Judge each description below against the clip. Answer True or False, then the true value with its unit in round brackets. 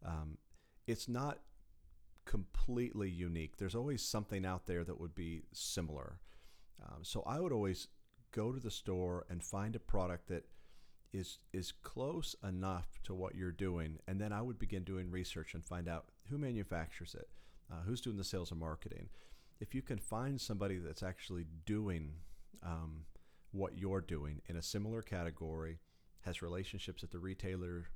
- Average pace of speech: True (165 wpm)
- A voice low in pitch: True (90 Hz)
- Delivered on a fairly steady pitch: False (3.8 semitones)